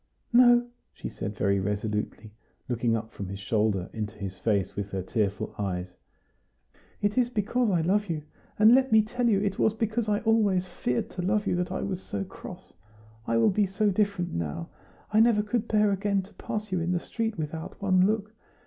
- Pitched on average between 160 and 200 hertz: Yes, medium, 185 Hz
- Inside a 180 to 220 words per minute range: Yes, average, 200 wpm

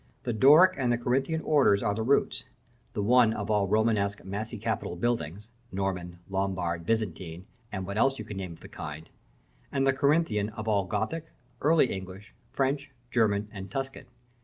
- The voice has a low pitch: Yes, low, 105 Hz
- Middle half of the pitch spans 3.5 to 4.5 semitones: No, wide, 5.4 semitones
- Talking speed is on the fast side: No, average, 170 wpm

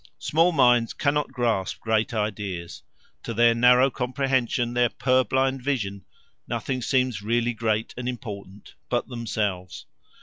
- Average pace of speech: No, slow, 125 wpm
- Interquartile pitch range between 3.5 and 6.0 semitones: No, average, 3.1 semitones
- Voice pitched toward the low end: Yes, low, 120 Hz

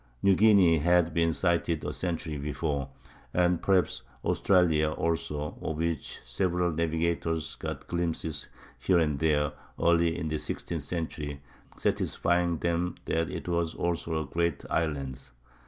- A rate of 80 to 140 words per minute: Yes, slow, 135 wpm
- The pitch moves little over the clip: Yes, narrow, 2.1 semitones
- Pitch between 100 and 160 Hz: No, very low, 80 Hz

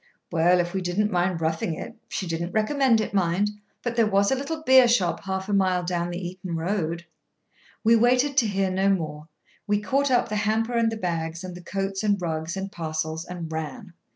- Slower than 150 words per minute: No, average, 200 wpm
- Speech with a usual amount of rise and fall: Yes, average, 4.0 semitones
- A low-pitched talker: No, high, 190 Hz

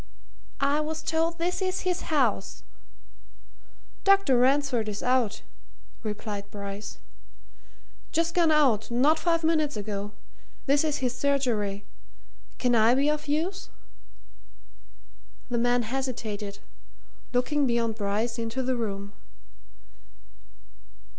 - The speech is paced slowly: Yes, slow, 110 wpm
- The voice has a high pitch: Yes, very high, 255 Hz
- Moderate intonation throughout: No, wide, 5.8 semitones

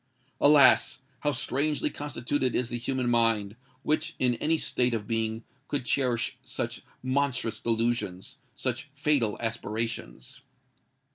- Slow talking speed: Yes, slow, 115 wpm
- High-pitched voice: No, low, 125 Hz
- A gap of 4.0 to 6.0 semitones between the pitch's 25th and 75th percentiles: No, average, 3.6 semitones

